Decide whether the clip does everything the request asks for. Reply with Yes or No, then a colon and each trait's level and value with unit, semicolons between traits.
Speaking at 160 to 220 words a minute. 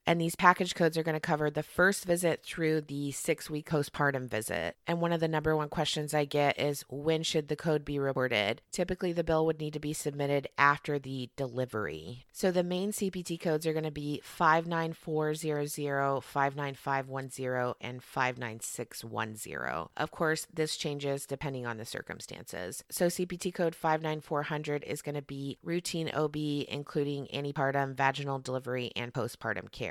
Yes: average, 165 wpm